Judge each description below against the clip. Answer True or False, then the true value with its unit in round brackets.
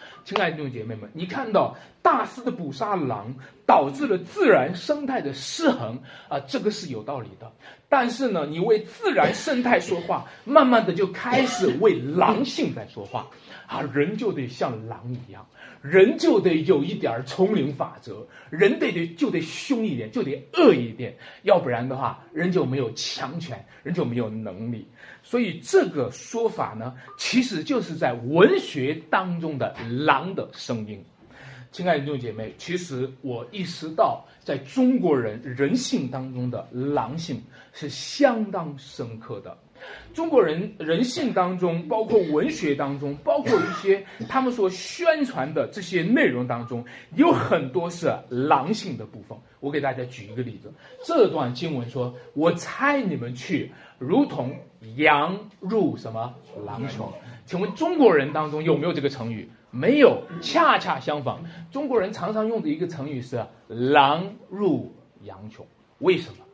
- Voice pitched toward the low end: False (155 Hz)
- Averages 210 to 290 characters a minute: True (235 characters per minute)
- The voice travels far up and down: True (8.8 semitones)